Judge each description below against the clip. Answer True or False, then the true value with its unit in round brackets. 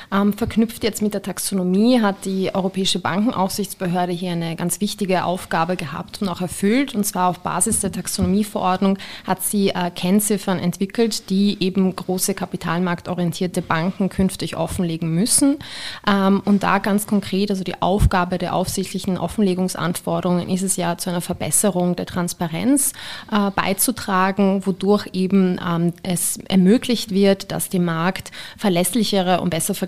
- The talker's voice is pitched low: False (190 Hz)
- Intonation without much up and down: True (2.1 semitones)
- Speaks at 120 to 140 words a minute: True (135 wpm)